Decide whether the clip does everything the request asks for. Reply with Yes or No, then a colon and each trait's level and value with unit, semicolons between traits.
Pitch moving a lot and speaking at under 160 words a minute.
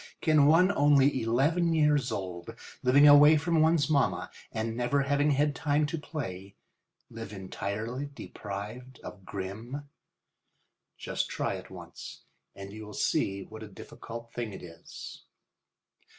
Yes: wide, 5.7 semitones; slow, 135 wpm